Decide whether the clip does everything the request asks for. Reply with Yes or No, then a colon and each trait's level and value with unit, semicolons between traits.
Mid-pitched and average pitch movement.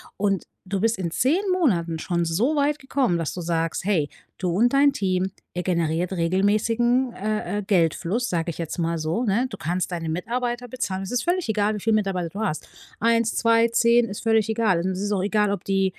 No: high, 200 Hz; average, 4.8 semitones